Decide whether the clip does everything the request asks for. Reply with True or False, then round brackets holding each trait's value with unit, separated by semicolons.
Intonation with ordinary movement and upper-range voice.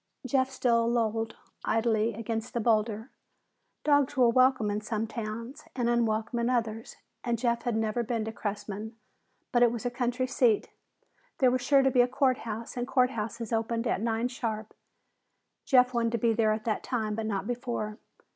False (1.9 semitones; 230 Hz)